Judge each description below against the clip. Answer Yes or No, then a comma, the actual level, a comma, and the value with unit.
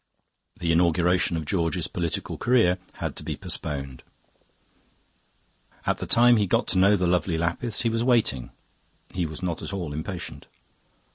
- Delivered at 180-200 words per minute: No, average, 155 wpm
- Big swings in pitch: No, average, 3.4 semitones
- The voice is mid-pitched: No, very low, 90 Hz